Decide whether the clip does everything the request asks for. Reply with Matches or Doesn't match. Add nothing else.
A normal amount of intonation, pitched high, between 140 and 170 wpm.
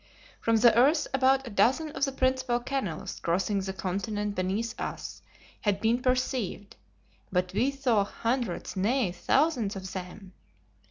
Matches